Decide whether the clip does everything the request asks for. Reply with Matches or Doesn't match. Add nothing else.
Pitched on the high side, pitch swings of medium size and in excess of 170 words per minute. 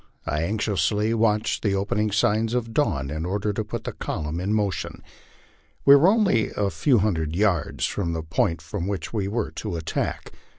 Doesn't match